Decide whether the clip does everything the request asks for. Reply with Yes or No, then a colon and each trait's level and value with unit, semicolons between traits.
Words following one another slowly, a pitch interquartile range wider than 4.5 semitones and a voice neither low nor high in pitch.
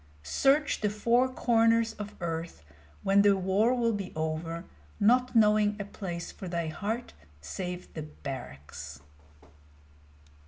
No: slow, 125 wpm; wide, 5.5 semitones; high, 200 Hz